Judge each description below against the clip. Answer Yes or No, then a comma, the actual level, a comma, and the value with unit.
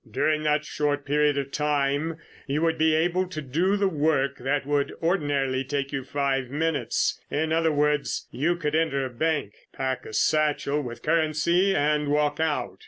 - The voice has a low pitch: No, medium, 150 Hz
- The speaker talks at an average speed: Yes, average, 170 wpm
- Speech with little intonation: Yes, narrow, 2.3 semitones